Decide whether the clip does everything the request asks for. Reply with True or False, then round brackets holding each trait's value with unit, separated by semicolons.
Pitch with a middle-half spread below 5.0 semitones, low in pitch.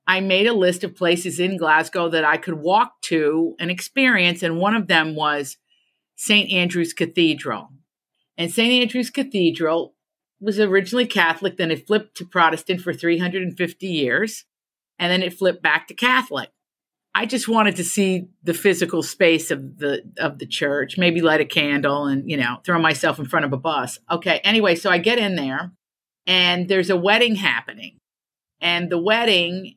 False (3.3 semitones; 175 Hz)